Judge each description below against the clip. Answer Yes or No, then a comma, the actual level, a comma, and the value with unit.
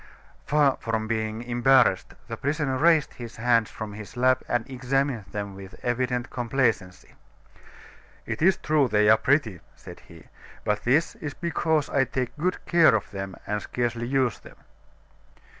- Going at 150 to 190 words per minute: Yes, average, 155 wpm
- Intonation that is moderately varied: Yes, average, 4.1 semitones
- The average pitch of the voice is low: Yes, low, 120 Hz